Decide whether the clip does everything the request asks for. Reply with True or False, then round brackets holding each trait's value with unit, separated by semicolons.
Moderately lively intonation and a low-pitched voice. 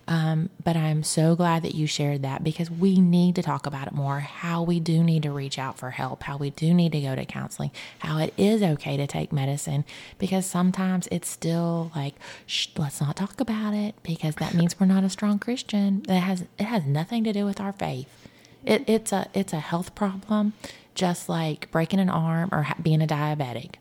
False (4.2 semitones; 165 Hz)